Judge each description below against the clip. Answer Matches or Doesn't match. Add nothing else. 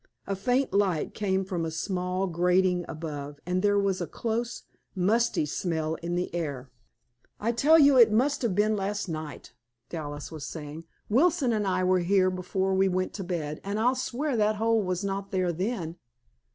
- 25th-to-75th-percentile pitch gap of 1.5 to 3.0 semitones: Doesn't match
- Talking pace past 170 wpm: Matches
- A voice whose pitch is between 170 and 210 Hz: Matches